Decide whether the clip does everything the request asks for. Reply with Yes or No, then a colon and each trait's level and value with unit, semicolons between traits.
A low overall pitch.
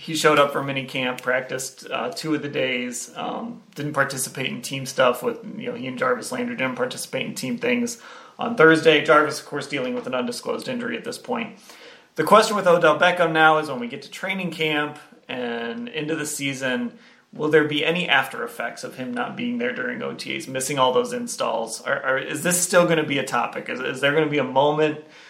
No: medium, 155 Hz